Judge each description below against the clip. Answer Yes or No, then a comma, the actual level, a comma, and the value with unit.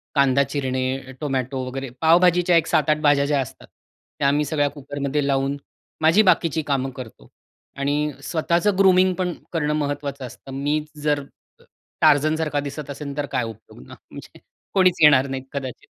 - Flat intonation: Yes, narrow, 2.3 semitones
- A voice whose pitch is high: No, medium, 145 Hz